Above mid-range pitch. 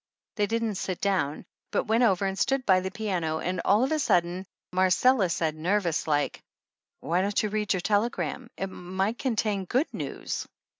Yes: high, 195 Hz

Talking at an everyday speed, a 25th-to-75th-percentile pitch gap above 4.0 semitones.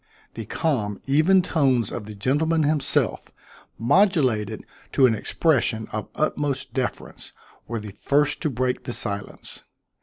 No: slow, 130 wpm; wide, 5.4 semitones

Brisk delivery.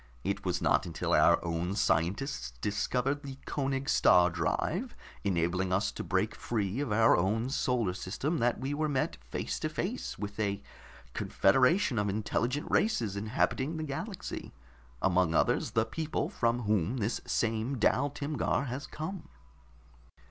No: average, 150 wpm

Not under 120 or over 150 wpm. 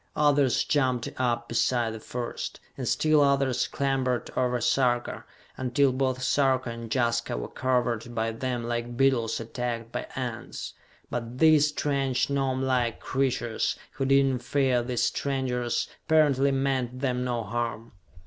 Yes: average, 140 wpm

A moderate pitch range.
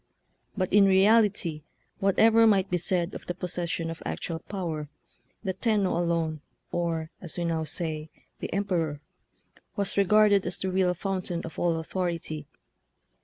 Yes: average, 3.0 semitones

